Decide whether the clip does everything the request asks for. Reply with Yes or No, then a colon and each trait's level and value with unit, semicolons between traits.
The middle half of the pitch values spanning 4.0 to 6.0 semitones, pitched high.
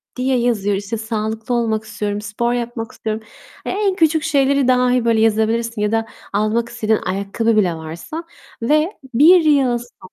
No: average, 2.9 semitones; high, 230 Hz